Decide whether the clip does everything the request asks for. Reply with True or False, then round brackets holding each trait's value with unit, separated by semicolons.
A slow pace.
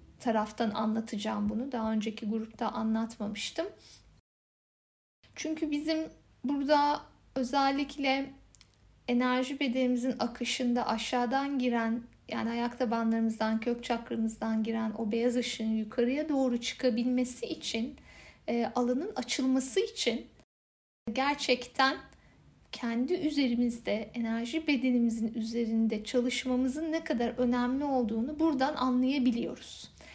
True (90 wpm)